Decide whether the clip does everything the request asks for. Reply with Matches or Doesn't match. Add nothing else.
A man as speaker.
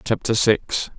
Matches